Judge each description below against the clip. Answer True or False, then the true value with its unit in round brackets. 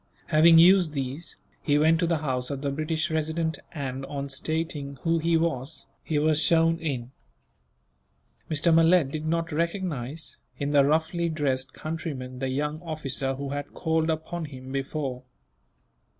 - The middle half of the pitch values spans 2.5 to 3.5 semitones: True (3.0 semitones)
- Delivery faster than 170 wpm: False (150 wpm)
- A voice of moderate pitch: True (155 Hz)